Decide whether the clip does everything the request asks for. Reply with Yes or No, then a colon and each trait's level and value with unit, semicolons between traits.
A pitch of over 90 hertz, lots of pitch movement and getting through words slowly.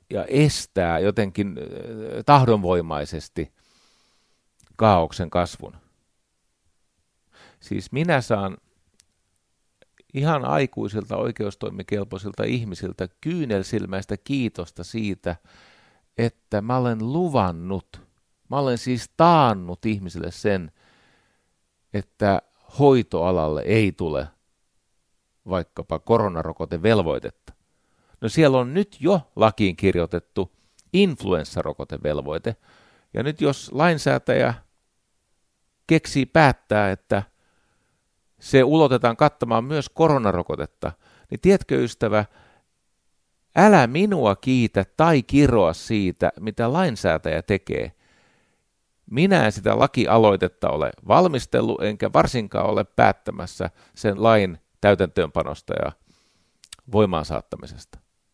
Yes: low, 105 Hz; wide, 6.0 semitones; slow, 85 wpm